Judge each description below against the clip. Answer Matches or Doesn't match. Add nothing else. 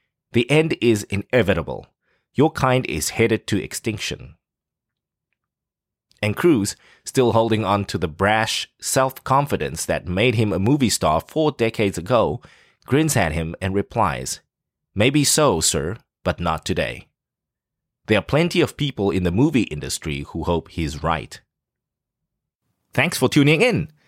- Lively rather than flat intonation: Matches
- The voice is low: Matches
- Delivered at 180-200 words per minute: Doesn't match